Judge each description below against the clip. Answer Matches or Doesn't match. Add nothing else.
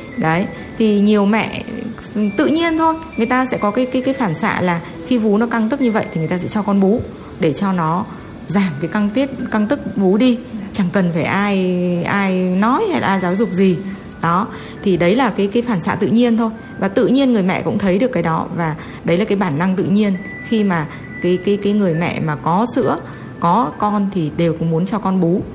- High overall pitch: Matches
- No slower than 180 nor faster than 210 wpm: Doesn't match